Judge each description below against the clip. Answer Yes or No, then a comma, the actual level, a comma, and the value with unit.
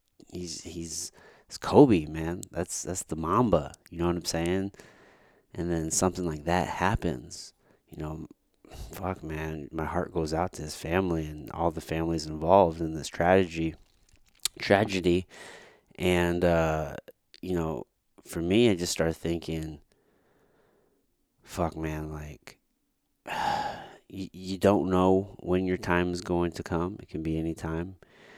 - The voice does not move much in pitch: Yes, narrow, 2.2 semitones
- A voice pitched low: Yes, very low, 85 Hz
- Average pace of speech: Yes, average, 145 wpm